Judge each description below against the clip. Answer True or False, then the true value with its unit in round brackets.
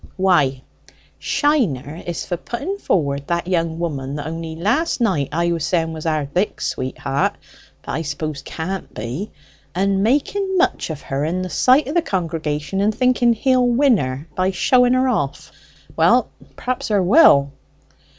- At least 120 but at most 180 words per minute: True (165 wpm)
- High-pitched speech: False (175 Hz)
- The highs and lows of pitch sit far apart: True (8.0 semitones)